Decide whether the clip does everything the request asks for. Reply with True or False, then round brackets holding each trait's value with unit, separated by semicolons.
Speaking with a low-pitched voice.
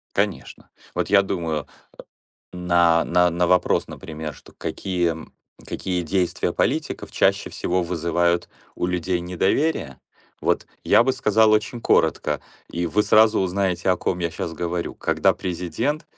True (90 Hz)